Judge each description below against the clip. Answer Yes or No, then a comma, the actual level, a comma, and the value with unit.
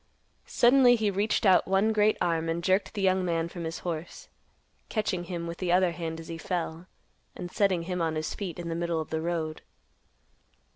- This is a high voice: No, medium, 175 Hz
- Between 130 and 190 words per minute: No, average, 200 wpm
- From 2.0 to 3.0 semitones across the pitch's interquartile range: Yes, narrow, 2.6 semitones